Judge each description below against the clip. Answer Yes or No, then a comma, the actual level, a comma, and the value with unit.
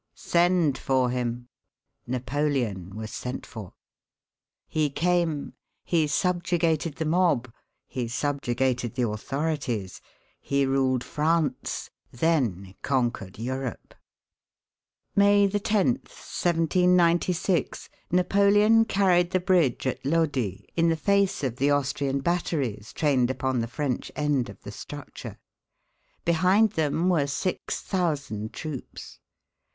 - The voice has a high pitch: No, medium, 145 Hz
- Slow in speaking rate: Yes, slow, 105 wpm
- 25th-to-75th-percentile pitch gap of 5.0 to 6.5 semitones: Yes, wide, 5.6 semitones